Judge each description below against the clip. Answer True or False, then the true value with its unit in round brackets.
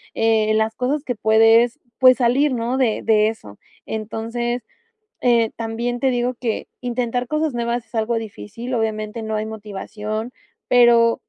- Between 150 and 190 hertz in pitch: False (230 Hz)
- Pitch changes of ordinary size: False (2.0 semitones)